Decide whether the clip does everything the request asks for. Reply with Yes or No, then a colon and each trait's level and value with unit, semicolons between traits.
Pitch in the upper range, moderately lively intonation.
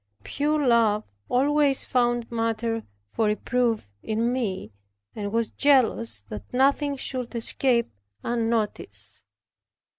Yes: high, 235 Hz; average, 3.2 semitones